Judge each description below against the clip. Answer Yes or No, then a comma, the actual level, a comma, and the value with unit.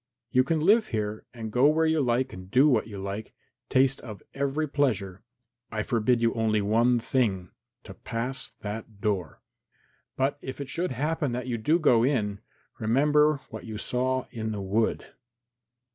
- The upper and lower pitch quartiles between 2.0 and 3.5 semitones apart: No, average, 4.2 semitones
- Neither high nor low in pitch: No, low, 120 Hz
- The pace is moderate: Yes, average, 170 wpm